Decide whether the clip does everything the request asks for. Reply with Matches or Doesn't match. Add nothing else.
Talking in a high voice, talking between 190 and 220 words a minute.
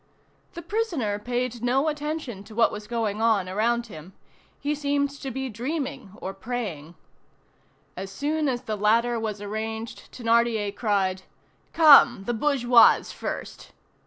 Doesn't match